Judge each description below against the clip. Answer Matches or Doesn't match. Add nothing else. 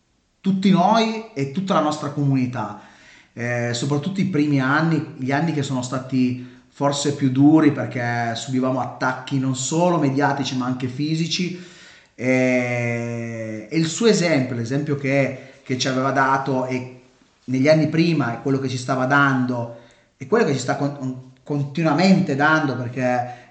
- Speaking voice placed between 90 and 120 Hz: Doesn't match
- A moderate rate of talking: Matches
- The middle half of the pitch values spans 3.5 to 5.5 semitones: Doesn't match